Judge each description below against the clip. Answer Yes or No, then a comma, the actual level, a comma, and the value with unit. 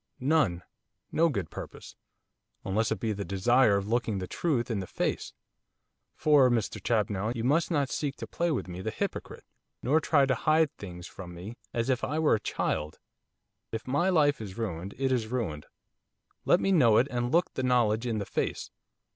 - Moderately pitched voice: No, low, 120 Hz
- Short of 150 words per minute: No, average, 190 wpm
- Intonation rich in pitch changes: Yes, wide, 5.8 semitones